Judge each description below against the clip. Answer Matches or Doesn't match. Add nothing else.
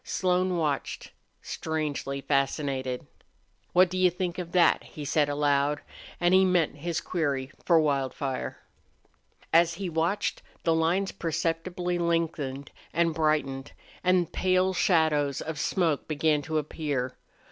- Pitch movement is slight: Doesn't match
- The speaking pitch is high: Doesn't match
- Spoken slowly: Matches